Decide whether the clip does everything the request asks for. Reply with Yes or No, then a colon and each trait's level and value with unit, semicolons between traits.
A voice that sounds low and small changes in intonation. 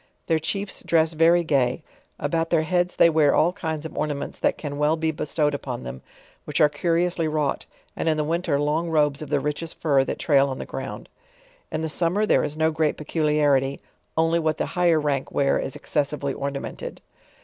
No: medium, 155 Hz; narrow, 2.3 semitones